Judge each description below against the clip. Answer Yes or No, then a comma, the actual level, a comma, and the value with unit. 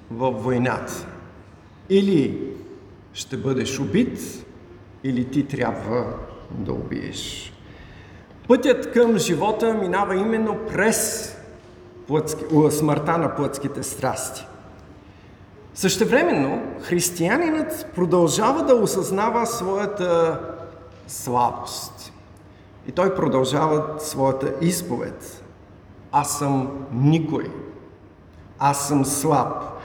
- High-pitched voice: No, medium, 140 Hz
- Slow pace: Yes, slow, 80 wpm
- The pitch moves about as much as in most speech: No, wide, 8.3 semitones